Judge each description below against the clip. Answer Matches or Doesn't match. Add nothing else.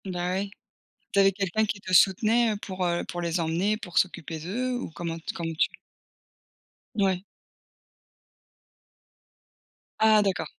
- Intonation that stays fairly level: Doesn't match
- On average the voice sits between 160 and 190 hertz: Matches